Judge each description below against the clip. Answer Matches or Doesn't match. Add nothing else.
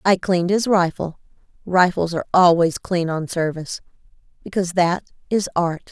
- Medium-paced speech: Doesn't match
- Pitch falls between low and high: Matches